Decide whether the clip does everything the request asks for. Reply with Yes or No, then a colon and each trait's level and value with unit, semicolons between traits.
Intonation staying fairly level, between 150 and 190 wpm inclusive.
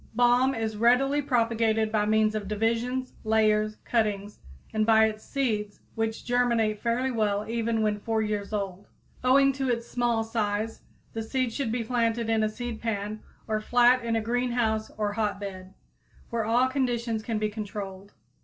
Yes: narrow, 2.0 semitones; average, 165 wpm